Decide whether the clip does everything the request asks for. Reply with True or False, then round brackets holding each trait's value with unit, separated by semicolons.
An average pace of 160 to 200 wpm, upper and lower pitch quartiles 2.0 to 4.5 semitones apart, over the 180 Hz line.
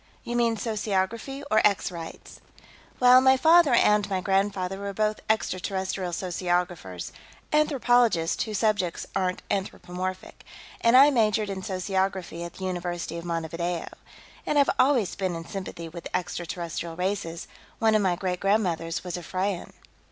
False (145 wpm; 3.6 semitones; 190 Hz)